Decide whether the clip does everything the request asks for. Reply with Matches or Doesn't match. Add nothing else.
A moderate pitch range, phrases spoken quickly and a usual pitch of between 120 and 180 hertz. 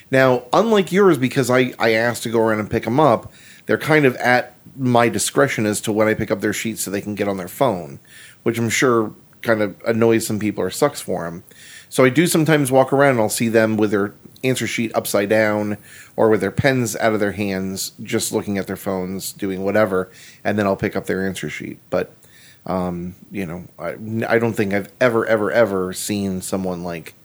Doesn't match